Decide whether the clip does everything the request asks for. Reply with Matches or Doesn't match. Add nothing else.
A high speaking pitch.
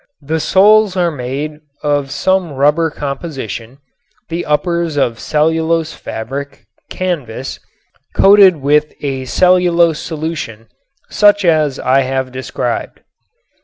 Doesn't match